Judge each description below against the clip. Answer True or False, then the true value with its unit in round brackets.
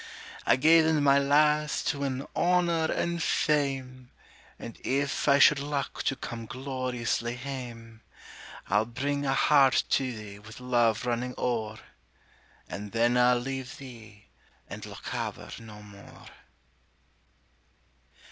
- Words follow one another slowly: True (125 wpm)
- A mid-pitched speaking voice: False (130 Hz)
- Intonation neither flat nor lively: True (3.4 semitones)